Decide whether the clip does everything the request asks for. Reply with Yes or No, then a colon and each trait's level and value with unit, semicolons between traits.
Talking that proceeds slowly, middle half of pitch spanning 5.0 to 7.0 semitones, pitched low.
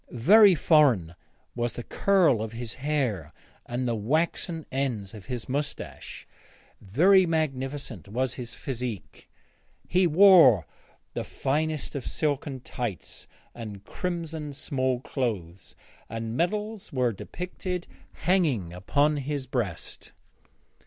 Yes: slow, 110 wpm; wide, 5.6 semitones; low, 130 Hz